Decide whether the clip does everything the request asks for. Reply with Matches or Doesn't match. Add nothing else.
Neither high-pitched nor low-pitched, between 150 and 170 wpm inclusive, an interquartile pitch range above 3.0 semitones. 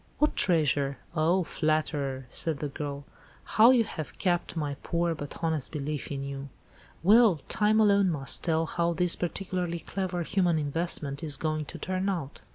Matches